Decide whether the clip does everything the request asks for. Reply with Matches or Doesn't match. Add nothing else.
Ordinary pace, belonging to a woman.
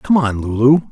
Doesn't match